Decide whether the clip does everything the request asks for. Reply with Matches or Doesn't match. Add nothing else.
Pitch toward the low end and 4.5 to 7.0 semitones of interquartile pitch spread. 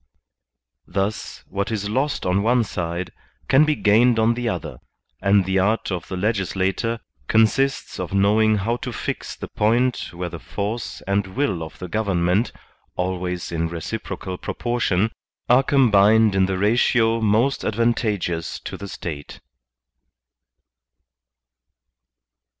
Doesn't match